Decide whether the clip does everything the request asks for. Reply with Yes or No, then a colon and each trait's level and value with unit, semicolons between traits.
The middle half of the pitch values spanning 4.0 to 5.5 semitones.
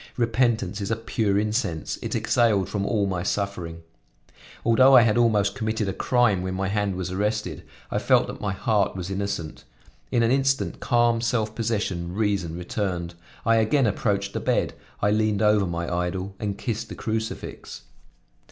No: average, 3.0 semitones